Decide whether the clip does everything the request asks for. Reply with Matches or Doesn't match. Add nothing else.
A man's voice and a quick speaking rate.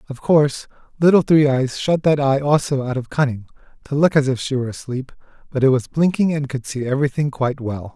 Matches